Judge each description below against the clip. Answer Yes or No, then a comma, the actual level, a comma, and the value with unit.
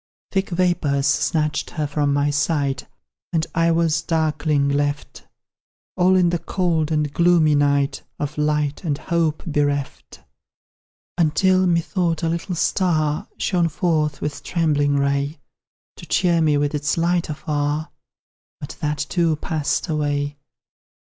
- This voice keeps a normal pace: No, slow, 130 wpm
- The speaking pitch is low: No, medium, 155 Hz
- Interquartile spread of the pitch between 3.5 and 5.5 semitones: No, narrow, 2.6 semitones